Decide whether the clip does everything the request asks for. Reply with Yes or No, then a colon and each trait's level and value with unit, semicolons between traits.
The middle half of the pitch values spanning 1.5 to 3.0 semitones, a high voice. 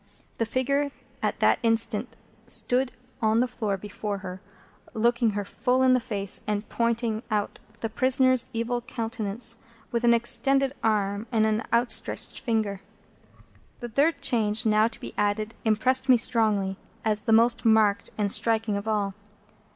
Yes: narrow, 2.4 semitones; high, 225 Hz